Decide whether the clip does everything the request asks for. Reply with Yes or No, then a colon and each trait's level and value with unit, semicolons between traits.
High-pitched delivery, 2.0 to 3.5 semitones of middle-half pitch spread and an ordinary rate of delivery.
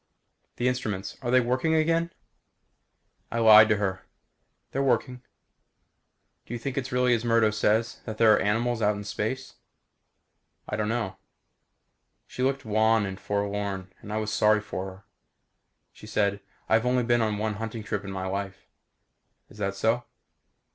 No: low, 110 Hz; average, 3.0 semitones; average, 160 wpm